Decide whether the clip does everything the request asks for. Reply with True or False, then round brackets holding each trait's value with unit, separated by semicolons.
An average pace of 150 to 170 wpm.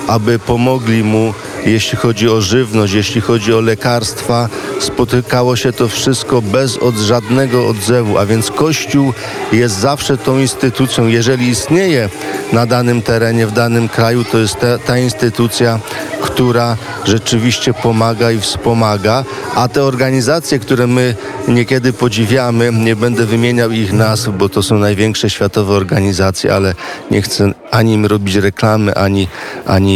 False (140 wpm)